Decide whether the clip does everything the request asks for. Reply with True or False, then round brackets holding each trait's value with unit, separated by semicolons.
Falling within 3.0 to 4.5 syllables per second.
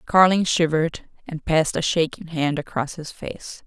False (4.8 syllables/s)